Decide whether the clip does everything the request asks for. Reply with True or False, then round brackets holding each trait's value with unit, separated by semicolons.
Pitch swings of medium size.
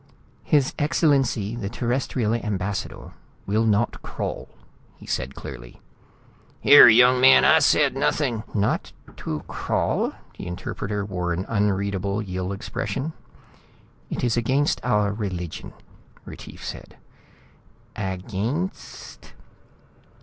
True (4.6 semitones)